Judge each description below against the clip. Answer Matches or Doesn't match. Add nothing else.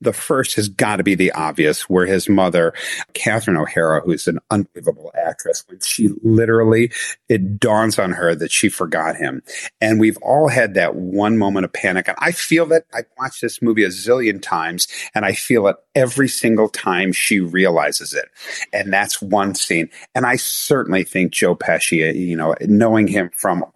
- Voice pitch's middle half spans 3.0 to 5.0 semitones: Matches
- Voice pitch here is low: Matches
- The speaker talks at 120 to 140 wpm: Doesn't match